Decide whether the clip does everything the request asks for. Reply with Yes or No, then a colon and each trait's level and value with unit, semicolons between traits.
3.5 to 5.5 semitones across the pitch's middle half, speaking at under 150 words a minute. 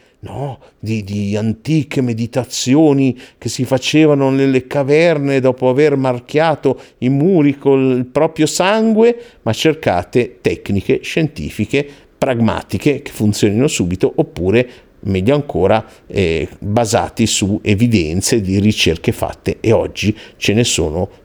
Yes: average, 4.9 semitones; slow, 115 wpm